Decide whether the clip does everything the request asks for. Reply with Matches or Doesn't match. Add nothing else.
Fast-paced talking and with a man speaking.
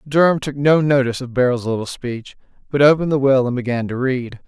Matches